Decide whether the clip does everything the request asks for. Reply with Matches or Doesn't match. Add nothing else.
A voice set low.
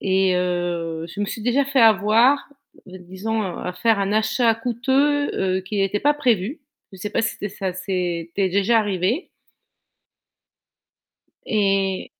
Doesn't match